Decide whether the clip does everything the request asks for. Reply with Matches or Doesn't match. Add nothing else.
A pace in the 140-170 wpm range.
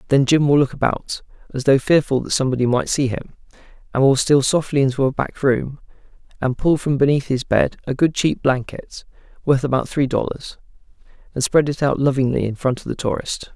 Doesn't match